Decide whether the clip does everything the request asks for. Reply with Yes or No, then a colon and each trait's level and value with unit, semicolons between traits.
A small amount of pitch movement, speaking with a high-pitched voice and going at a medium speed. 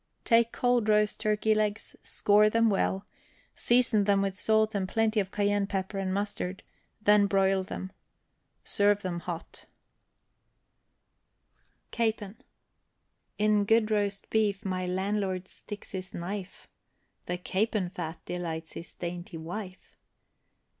No: narrow, 2.2 semitones; high, 200 Hz; slow, 120 wpm